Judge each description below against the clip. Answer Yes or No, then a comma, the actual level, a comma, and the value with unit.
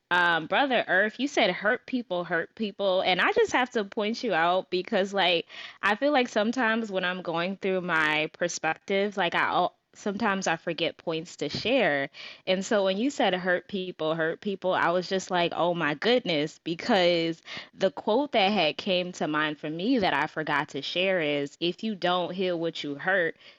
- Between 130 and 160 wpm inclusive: No, average, 195 wpm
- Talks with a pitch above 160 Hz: Yes, medium, 185 Hz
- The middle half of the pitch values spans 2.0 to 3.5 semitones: No, average, 3.9 semitones